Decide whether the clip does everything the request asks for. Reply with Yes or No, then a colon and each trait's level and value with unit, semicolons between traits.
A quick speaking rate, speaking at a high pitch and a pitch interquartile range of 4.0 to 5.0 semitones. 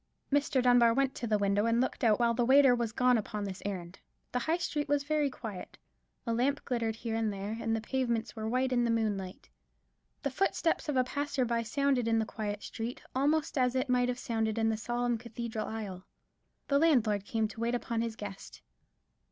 No: fast, 210 wpm; high, 235 Hz; average, 2.8 semitones